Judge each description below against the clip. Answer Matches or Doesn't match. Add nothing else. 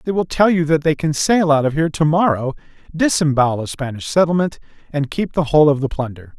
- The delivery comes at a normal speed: Doesn't match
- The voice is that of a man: Matches